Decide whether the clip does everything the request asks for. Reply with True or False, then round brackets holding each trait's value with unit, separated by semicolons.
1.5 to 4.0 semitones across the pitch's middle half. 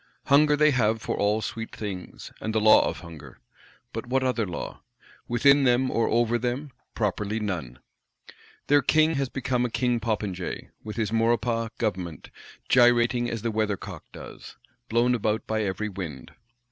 True (2.8 semitones)